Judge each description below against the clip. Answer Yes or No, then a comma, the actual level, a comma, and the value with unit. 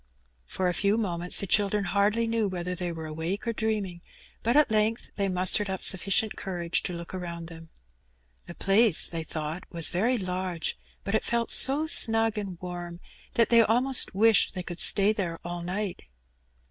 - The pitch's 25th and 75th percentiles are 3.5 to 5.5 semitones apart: Yes, average, 3.9 semitones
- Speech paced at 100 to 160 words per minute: No, average, 180 wpm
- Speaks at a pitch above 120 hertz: Yes, high, 190 Hz